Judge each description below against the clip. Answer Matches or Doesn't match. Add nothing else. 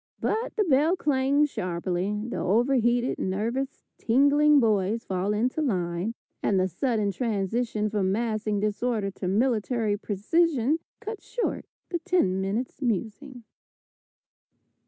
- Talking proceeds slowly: Matches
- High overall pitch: Matches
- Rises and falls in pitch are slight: Doesn't match